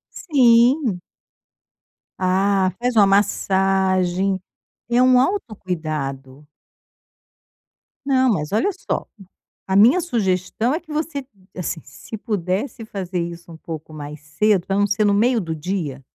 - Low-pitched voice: No, high, 195 Hz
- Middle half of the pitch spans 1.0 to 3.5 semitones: No, average, 5.1 semitones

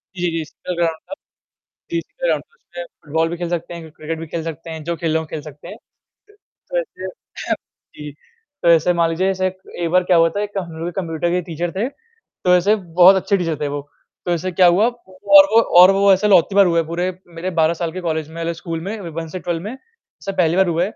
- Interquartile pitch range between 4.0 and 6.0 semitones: No, narrow, 2.6 semitones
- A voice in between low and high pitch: Yes, medium, 175 Hz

